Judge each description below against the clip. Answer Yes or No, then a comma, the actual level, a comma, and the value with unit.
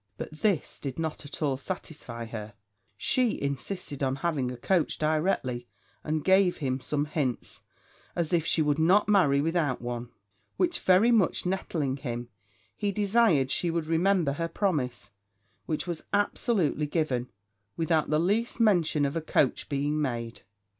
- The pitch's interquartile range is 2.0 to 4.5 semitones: No, average, 5.0 semitones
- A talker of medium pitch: Yes, medium, 155 Hz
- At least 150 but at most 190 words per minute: Yes, average, 155 wpm